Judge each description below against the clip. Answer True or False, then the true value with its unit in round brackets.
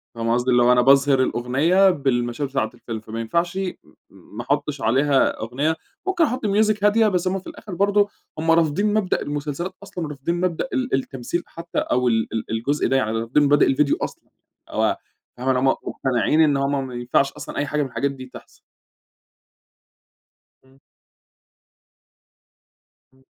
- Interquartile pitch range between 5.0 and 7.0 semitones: True (5.5 semitones)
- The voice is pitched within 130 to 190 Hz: True (140 Hz)